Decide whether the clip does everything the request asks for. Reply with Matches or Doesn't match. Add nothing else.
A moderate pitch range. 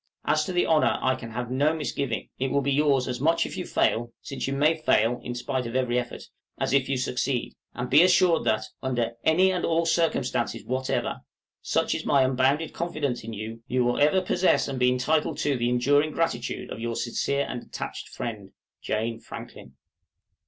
Matches